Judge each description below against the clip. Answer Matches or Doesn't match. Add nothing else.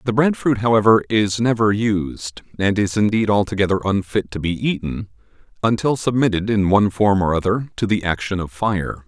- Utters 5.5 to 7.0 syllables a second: Doesn't match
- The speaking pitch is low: Matches